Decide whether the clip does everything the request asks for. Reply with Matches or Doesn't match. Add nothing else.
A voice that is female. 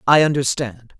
Matches